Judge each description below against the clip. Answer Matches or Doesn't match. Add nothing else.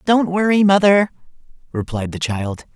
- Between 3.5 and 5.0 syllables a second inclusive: Matches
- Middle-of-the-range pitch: Matches